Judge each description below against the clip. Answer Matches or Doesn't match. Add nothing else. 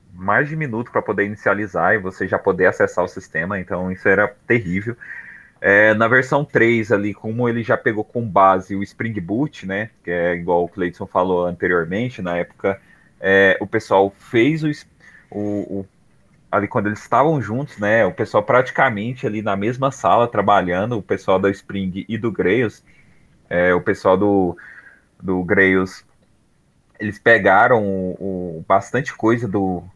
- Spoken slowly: Doesn't match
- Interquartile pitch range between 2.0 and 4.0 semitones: Matches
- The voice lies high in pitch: Doesn't match